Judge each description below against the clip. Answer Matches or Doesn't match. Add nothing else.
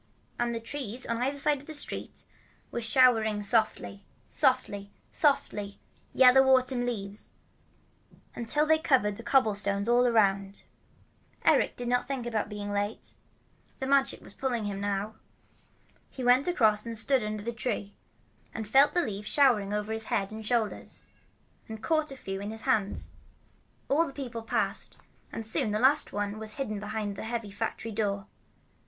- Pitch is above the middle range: Matches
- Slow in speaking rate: Doesn't match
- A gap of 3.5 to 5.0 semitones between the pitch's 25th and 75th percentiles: Matches